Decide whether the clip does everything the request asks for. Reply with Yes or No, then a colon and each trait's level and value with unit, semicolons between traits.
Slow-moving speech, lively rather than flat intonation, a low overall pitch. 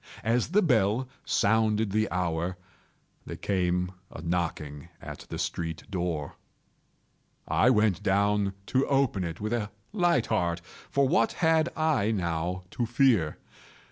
Yes: slow, 130 wpm; wide, 5.8 semitones; low, 100 Hz